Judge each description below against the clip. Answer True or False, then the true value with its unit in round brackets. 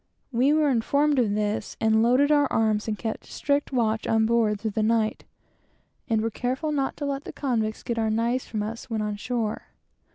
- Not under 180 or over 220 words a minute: True (200 wpm)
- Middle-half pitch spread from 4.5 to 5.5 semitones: False (3.5 semitones)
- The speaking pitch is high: True (230 Hz)